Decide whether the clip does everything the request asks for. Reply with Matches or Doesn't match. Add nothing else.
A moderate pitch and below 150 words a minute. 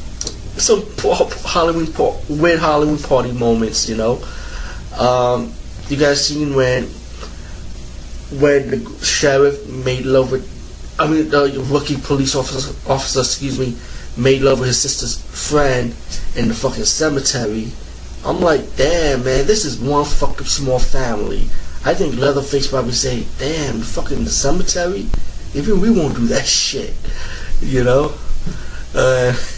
Doesn't match